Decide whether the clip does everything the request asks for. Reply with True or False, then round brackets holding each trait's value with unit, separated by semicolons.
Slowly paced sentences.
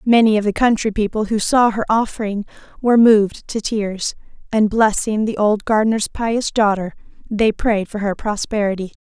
False (165 wpm)